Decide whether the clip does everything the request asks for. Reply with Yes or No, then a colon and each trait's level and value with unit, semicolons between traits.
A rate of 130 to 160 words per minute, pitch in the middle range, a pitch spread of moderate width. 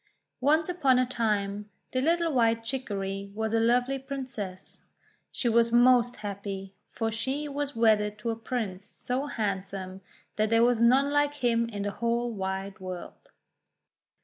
No: average, 150 wpm; high, 230 Hz; average, 4.0 semitones